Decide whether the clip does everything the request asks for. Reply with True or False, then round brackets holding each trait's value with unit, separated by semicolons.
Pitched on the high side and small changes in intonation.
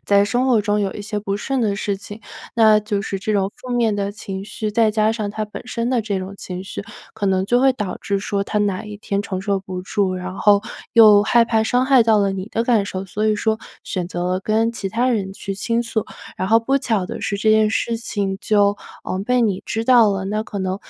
True (210 Hz; 2.3 semitones)